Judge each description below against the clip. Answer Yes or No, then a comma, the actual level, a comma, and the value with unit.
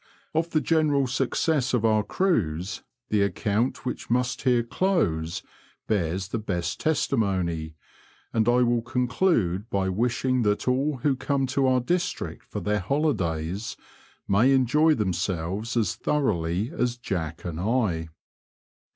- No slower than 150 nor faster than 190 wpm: No, slow, 135 wpm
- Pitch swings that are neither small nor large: No, wide, 6.0 semitones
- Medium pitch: No, low, 115 Hz